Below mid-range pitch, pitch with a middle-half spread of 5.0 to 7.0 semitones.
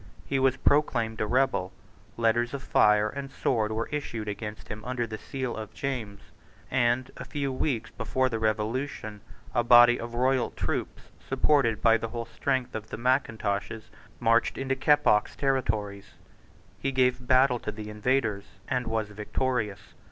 No: low, 120 Hz; average, 3.3 semitones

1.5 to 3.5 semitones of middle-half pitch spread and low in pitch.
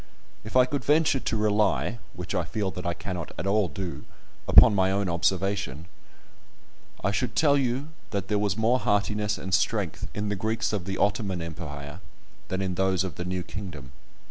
Yes: average, 2.9 semitones; low, 100 Hz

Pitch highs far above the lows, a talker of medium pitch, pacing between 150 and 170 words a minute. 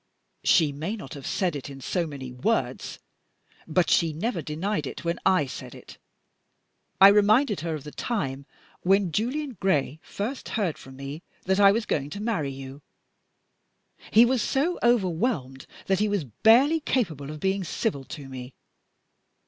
Yes: wide, 7.0 semitones; medium, 175 Hz; average, 165 wpm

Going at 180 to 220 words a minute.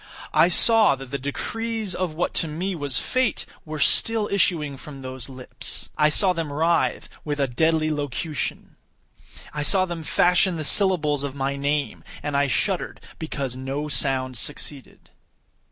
No: average, 155 wpm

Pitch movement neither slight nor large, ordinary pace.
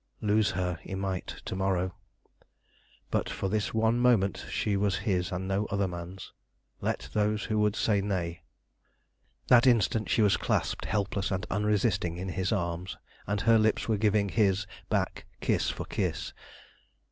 No: narrow, 2.3 semitones; average, 160 wpm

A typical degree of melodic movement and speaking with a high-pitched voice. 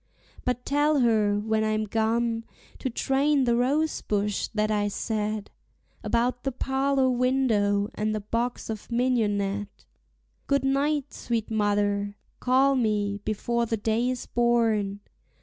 Yes: average, 3.4 semitones; high, 230 Hz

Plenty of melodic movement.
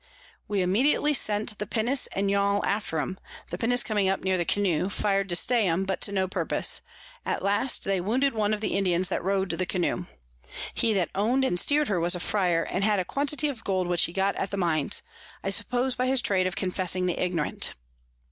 No: average, 3.1 semitones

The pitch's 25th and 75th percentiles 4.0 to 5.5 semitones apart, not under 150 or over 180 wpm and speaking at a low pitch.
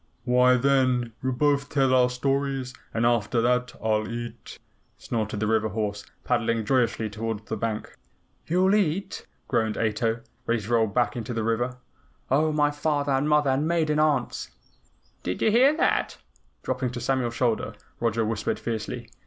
No: average, 3.6 semitones; average, 160 wpm; low, 125 Hz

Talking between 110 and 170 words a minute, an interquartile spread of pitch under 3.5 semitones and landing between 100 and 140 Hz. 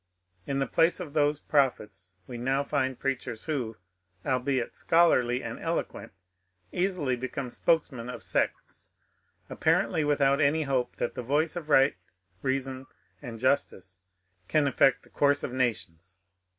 Yes: slow, 135 wpm; average, 2.9 semitones; low, 135 Hz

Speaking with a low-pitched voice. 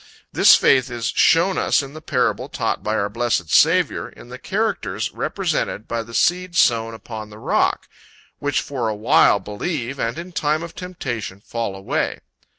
Yes: low, 120 Hz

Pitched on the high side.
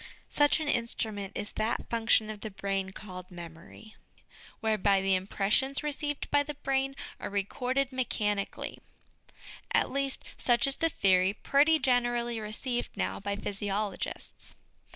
Yes: high, 220 Hz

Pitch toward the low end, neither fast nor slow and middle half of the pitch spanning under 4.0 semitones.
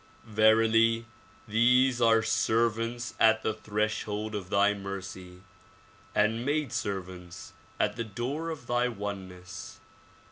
No: low, 110 Hz; slow, 110 wpm; average, 2.7 semitones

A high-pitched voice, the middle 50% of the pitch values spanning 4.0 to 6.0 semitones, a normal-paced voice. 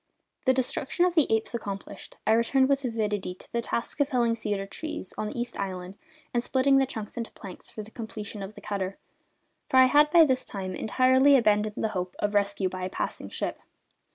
No: high, 225 Hz; average, 4.5 semitones; fast, 210 wpm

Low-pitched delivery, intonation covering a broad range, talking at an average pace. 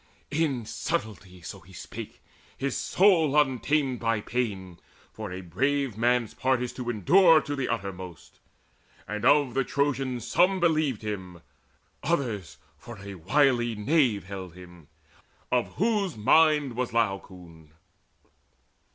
No: low, 120 Hz; wide, 6.6 semitones; slow, 125 wpm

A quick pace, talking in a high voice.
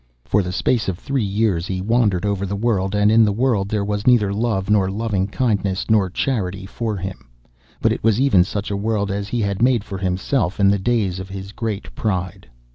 No: fast, 215 wpm; low, 100 Hz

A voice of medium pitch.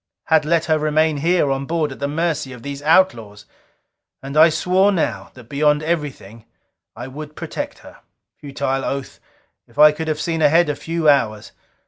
Yes: medium, 150 Hz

